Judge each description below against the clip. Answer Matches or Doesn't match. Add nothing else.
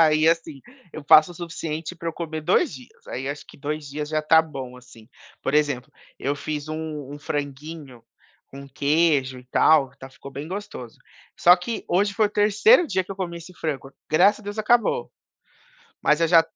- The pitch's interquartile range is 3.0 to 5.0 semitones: Matches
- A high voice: Doesn't match